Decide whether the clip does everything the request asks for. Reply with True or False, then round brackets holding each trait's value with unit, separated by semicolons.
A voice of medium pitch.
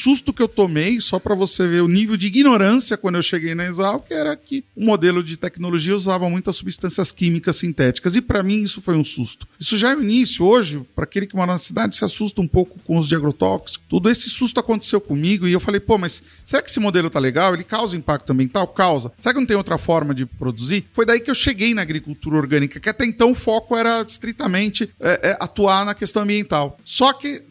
False (195 Hz)